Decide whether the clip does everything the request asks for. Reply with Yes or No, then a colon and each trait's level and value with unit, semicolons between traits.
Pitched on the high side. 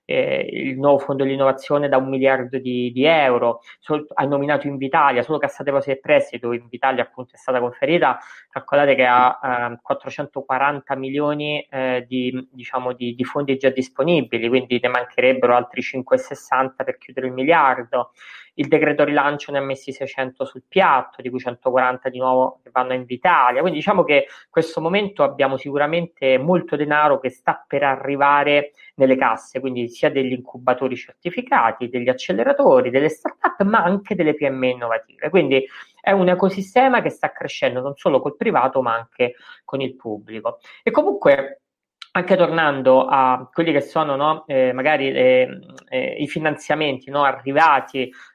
No: low, 135 Hz